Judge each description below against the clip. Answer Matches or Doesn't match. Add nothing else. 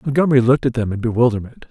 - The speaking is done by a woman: Doesn't match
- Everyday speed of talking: Doesn't match